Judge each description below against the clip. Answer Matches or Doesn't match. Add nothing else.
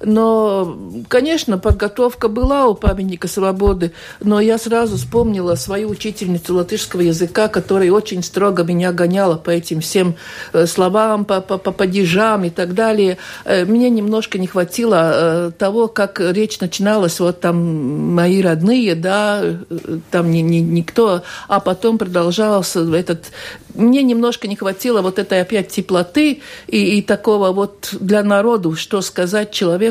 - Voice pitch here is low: Doesn't match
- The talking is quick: Doesn't match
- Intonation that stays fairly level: Doesn't match